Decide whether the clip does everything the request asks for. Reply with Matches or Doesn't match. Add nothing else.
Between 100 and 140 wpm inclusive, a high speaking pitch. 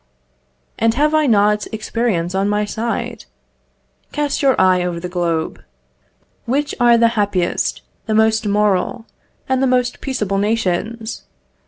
Matches